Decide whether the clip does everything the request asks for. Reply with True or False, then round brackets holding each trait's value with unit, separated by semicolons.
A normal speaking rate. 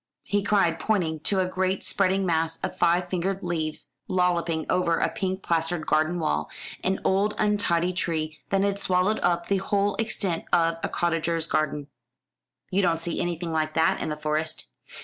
True (170 wpm)